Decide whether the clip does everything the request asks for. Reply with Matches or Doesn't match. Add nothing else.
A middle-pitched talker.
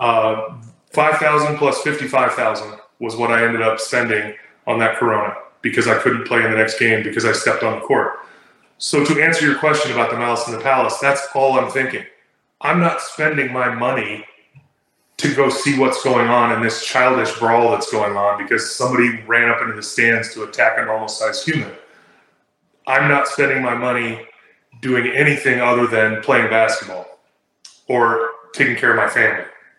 Doesn't match